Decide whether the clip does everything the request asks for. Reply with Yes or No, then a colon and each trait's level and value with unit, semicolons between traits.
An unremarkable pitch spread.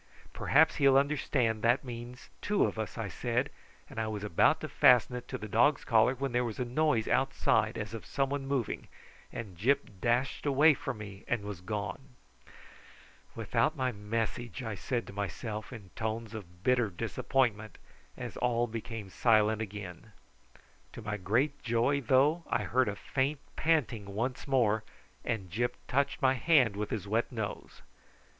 Yes: average, 3.8 semitones